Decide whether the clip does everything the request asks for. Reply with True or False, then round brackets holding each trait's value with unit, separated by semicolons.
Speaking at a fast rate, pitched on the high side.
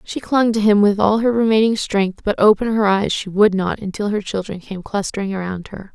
True (230 wpm; 205 Hz)